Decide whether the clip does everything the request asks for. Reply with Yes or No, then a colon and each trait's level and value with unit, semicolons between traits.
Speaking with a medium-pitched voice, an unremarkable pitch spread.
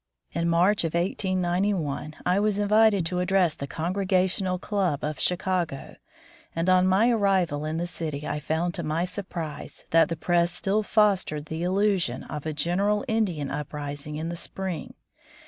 Yes: medium, 175 Hz; average, 3.7 semitones